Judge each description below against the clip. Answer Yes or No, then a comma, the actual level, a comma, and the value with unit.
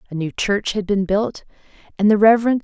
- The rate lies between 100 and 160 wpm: No, fast, 205 wpm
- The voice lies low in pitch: No, high, 205 Hz